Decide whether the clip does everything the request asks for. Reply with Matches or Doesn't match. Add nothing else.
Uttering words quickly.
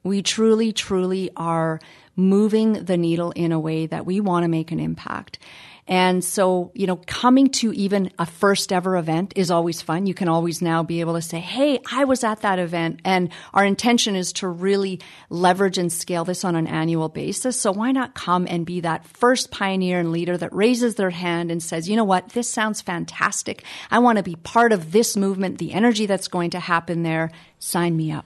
Matches